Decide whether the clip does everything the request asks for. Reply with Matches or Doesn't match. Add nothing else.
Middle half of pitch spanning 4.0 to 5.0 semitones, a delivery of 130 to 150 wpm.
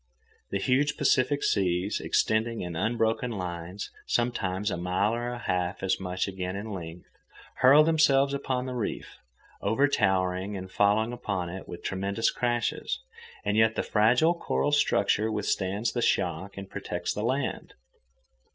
Matches